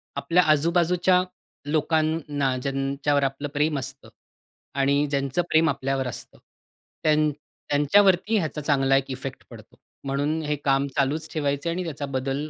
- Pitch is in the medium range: Yes, medium, 145 Hz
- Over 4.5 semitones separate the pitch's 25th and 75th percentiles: No, narrow, 2.5 semitones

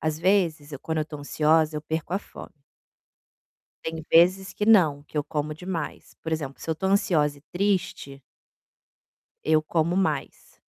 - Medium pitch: Yes, medium, 160 Hz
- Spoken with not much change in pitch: No, average, 3.0 semitones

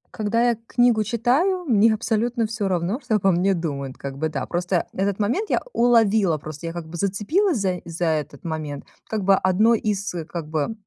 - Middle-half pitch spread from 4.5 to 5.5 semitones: Yes, average, 5.2 semitones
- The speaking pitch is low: No, high, 200 Hz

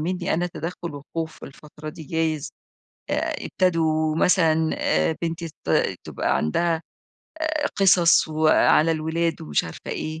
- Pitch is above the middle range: No, medium, 160 Hz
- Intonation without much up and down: Yes, narrow, 1.6 semitones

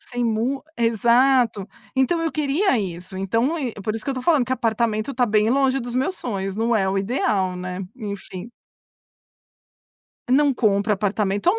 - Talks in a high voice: Yes, high, 230 Hz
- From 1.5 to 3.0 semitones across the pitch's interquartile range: No, average, 4.6 semitones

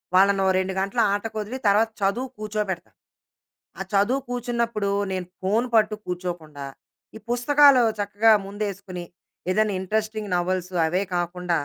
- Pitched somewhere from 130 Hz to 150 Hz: No, high, 205 Hz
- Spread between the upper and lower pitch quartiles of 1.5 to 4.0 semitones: Yes, average, 3.1 semitones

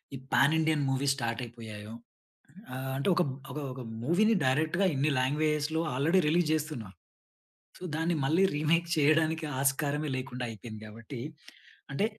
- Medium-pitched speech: Yes, medium, 145 Hz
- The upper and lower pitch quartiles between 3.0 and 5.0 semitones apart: Yes, average, 3.7 semitones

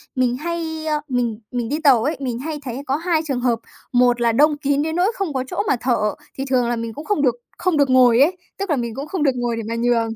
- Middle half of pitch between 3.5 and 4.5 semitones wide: Yes, average, 4.2 semitones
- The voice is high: Yes, very high, 265 Hz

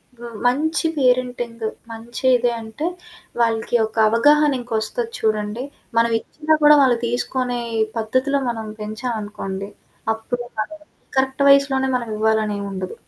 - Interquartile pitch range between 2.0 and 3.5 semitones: Yes, average, 3.1 semitones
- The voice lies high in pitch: Yes, high, 240 Hz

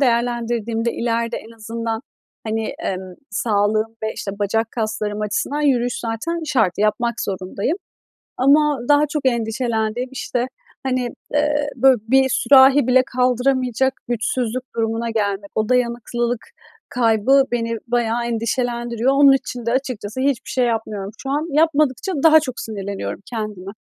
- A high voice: Yes, high, 235 Hz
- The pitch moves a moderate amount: Yes, average, 3.0 semitones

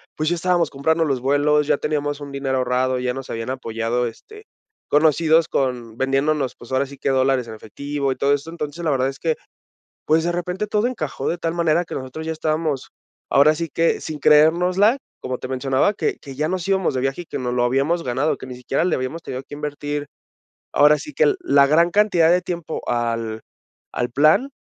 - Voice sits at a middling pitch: Yes, medium, 145 Hz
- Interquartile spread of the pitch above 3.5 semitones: Yes, average, 4.1 semitones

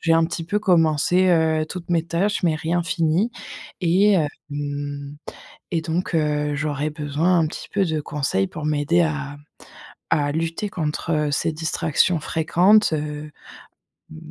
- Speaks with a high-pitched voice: No, medium, 160 Hz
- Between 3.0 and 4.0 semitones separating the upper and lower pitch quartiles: No, narrow, 2.5 semitones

